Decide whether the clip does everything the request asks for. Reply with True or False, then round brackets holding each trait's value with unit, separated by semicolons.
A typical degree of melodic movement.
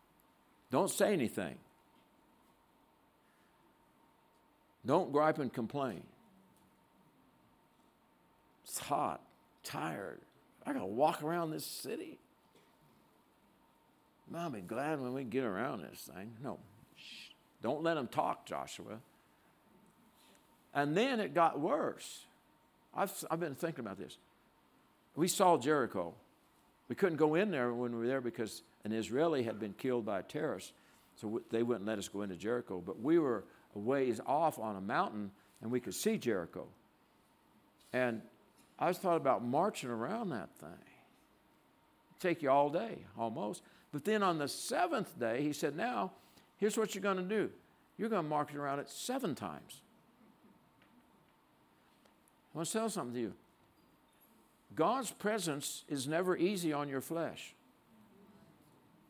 False (6.4 semitones)